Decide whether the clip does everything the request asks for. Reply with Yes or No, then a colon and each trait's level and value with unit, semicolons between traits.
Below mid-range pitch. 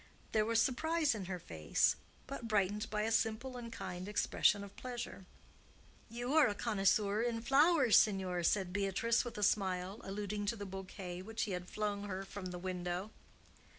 No: high, 205 Hz